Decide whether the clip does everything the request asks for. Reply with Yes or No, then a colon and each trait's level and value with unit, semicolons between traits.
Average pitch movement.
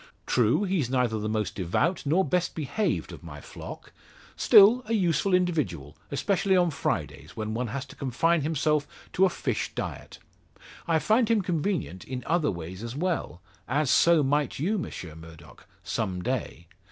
No: wide, 8.0 semitones